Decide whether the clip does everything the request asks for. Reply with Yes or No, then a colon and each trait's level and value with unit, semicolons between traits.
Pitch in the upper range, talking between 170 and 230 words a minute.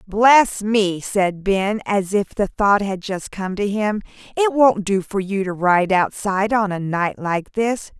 Yes: high, 200 Hz; average, 195 wpm